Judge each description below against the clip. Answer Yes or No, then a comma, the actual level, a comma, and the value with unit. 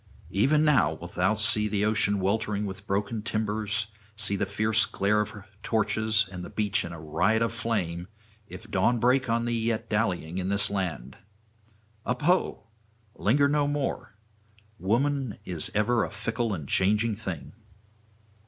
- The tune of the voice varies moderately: Yes, average, 3.0 semitones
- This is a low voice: Yes, low, 105 Hz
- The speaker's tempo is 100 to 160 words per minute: Yes, average, 155 wpm